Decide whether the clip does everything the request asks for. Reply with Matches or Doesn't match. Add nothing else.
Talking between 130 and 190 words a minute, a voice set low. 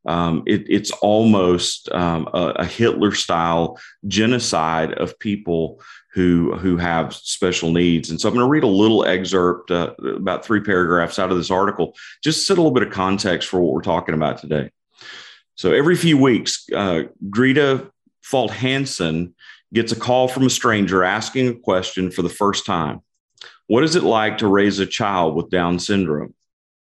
Matches